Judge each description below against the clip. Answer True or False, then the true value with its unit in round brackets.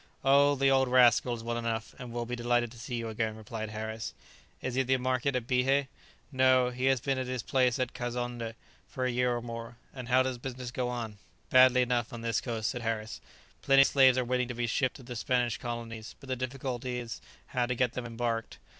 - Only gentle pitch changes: True (1.7 semitones)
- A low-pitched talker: True (125 Hz)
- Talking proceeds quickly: True (230 wpm)